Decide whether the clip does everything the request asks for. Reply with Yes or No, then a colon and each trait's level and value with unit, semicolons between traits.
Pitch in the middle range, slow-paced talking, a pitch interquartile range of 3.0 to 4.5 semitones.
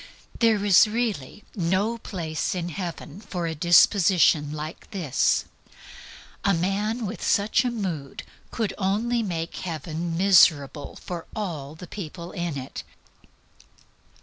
Yes: medium, 180 Hz; slow, 120 wpm; average, 4.2 semitones